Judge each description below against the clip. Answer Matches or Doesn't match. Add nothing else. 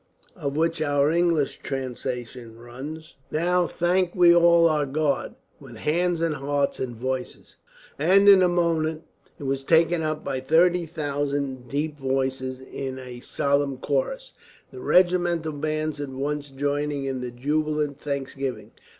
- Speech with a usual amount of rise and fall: Matches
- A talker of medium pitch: Matches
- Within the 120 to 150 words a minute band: Matches